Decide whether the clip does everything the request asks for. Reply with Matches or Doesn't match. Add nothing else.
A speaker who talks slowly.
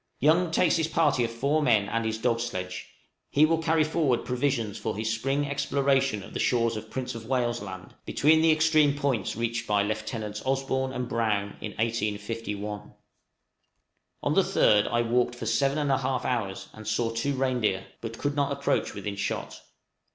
Doesn't match